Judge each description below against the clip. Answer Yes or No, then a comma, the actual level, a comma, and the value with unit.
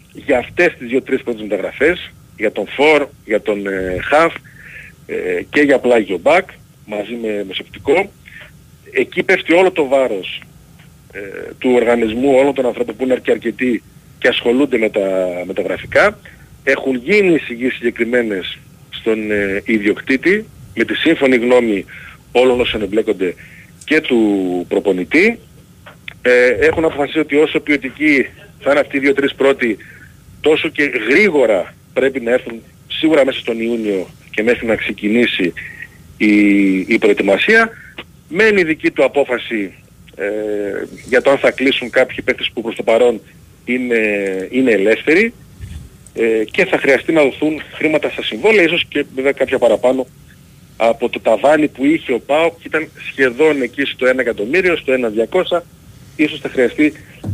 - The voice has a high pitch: No, low, 130 Hz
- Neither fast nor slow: Yes, average, 140 wpm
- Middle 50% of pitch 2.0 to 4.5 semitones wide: No, average, 5.2 semitones